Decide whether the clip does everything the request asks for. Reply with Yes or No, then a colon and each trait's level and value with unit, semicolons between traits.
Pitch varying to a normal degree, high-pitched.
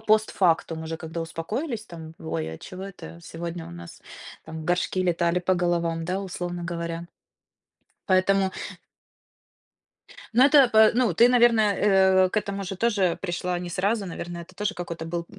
No: average, 3.0 semitones; medium, 180 Hz